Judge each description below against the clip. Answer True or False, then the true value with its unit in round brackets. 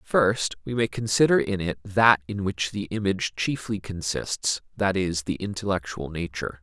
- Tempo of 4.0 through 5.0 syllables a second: True (4.7 syllables/s)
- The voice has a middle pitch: False (95 Hz)